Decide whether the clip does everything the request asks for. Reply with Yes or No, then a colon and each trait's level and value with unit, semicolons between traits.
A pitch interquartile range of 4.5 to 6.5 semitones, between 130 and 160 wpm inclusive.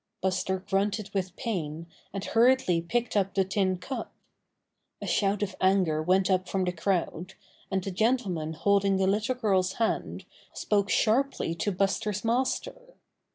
No: narrow, 2.6 semitones; average, 150 wpm